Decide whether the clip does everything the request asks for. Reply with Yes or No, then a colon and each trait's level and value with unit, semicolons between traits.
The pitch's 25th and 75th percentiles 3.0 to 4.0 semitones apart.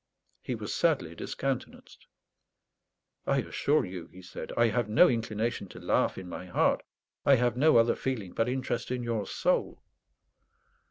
Yes: average, 3.6 semitones